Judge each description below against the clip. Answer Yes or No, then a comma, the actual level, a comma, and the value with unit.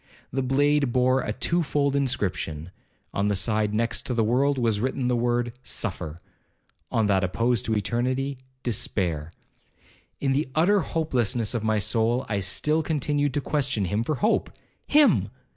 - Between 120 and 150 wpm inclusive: Yes, average, 145 wpm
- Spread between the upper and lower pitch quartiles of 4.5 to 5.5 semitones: Yes, average, 4.8 semitones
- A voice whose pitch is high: No, low, 120 Hz